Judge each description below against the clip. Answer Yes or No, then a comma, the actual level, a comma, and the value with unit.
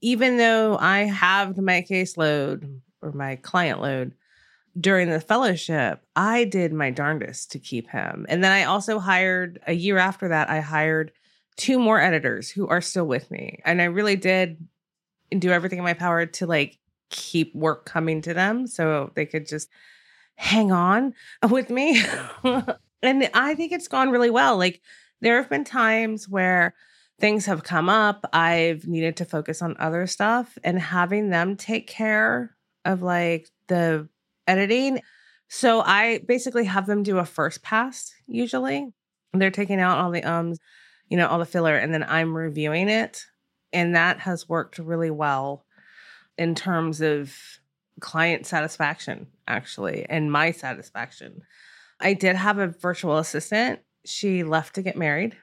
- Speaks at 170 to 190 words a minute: No, average, 160 wpm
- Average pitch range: Yes, average, 4.7 semitones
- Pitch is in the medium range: Yes, medium, 180 Hz